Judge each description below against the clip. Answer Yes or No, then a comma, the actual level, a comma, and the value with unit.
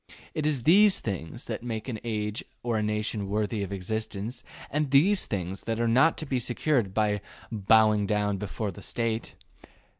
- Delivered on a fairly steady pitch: No, average, 3.0 semitones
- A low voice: Yes, low, 110 Hz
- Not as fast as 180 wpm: Yes, average, 170 wpm